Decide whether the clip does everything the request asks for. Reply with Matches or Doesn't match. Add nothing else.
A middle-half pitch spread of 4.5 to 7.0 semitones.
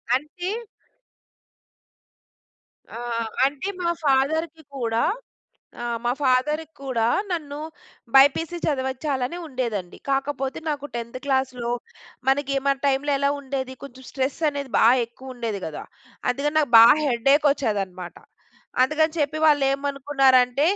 Doesn't match